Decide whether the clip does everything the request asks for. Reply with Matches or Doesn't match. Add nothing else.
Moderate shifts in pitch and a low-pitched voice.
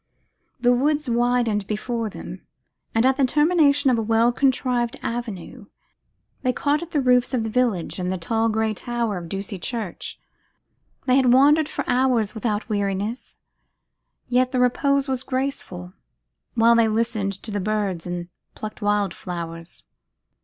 Doesn't match